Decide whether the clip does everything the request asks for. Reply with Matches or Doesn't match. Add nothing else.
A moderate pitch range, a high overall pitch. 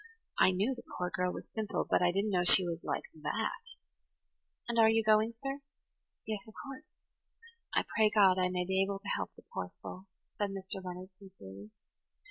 Matches